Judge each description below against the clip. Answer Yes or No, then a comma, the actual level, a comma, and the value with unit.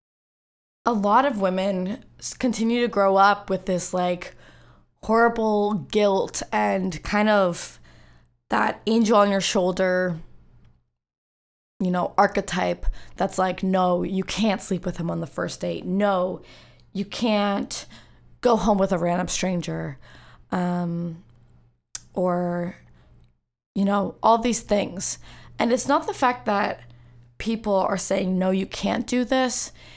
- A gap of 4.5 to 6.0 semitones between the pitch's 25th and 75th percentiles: No, average, 3.1 semitones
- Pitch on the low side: No, high, 190 Hz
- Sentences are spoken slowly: Yes, slow, 130 wpm